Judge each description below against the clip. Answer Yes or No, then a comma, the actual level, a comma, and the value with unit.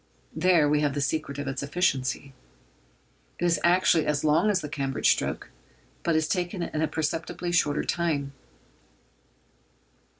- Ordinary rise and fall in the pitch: Yes, average, 3.2 semitones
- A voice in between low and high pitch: Yes, medium, 155 Hz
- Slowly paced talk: No, average, 145 wpm